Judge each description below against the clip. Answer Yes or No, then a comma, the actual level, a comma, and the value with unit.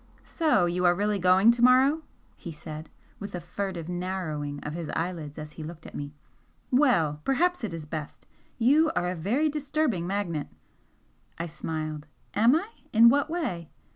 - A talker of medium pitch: Yes, medium, 180 Hz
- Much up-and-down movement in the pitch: Yes, wide, 7.7 semitones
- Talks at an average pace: Yes, average, 170 wpm